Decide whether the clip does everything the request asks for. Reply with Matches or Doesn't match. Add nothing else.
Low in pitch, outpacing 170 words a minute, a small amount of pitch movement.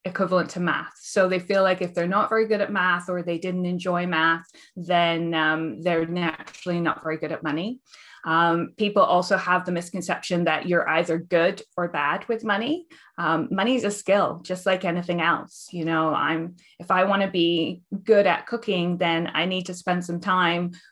Doesn't match